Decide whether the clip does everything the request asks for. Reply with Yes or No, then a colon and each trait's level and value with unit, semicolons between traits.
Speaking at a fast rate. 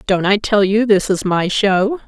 Yes: fast, 230 wpm